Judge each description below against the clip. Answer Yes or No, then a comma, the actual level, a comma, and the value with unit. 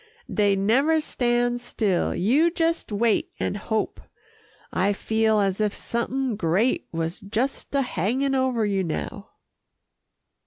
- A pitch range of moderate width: Yes, average, 4.6 semitones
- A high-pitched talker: Yes, high, 220 Hz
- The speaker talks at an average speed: No, slow, 125 wpm